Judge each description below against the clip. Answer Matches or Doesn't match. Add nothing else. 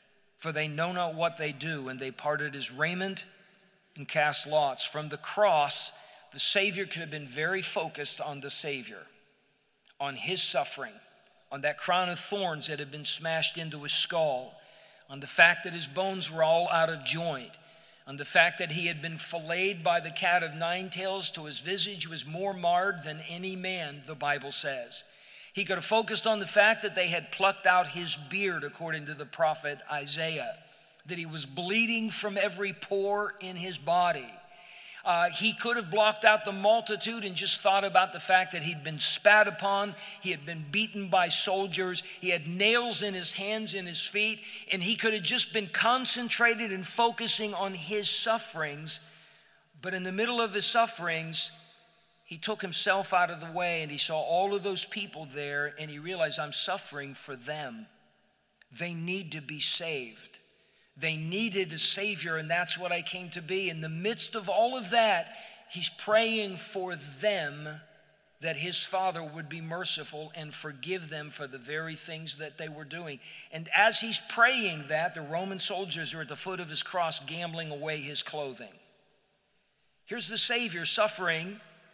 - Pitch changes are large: Doesn't match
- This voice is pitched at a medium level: Matches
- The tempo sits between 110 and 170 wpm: Doesn't match